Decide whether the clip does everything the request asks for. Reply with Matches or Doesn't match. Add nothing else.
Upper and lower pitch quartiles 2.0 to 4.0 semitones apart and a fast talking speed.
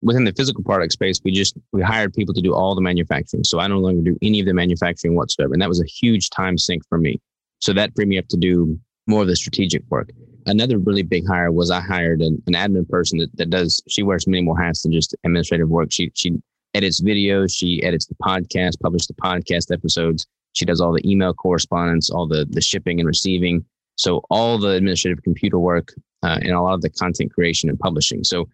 Matches